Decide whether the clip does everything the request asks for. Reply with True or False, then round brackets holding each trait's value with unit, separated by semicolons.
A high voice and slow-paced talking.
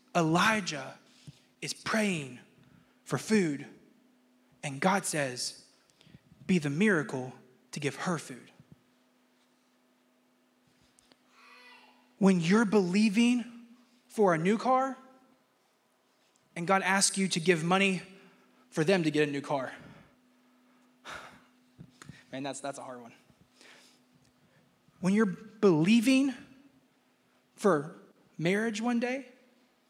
True (195 Hz; 100 wpm)